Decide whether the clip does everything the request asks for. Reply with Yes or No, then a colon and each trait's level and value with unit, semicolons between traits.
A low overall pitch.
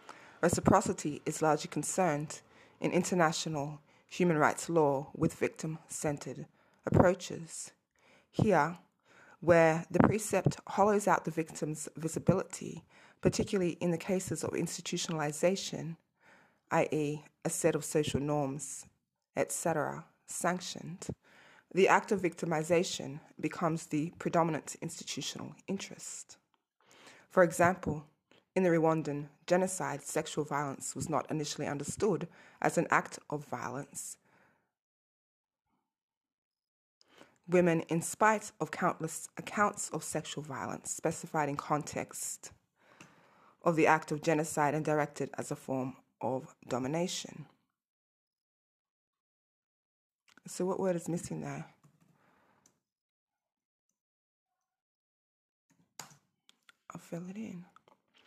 No: medium, 160 Hz